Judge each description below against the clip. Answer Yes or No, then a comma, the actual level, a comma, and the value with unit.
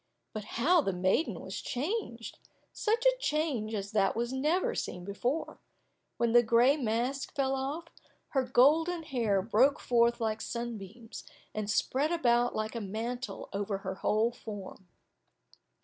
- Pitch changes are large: No, average, 4.5 semitones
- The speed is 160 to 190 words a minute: No, average, 145 wpm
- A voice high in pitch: Yes, high, 240 Hz